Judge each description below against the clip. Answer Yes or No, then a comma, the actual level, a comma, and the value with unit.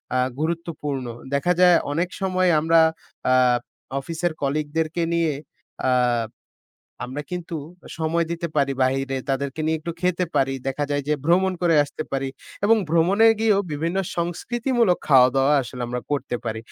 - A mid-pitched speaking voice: Yes, medium, 160 Hz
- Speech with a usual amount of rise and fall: Yes, average, 4.1 semitones